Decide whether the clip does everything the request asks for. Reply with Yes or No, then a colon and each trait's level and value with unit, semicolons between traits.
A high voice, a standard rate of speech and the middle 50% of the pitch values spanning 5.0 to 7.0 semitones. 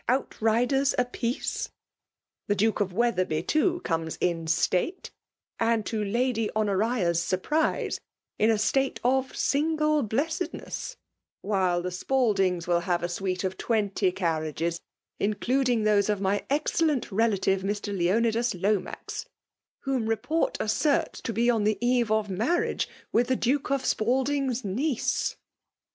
No: high, 220 Hz; slow, 125 wpm; average, 5.3 semitones